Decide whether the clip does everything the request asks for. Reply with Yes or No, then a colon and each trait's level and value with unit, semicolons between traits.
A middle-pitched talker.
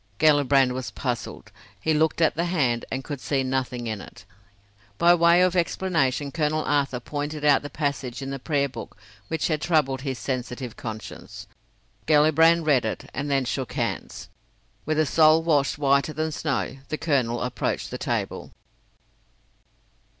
Yes: medium, 145 Hz